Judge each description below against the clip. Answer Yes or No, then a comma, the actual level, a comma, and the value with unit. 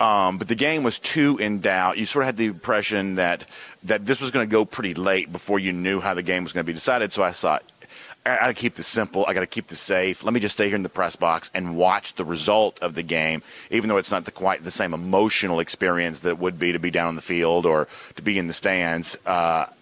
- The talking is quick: Yes, fast, 280 wpm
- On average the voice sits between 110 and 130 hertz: No, very low, 95 Hz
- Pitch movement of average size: Yes, average, 3.2 semitones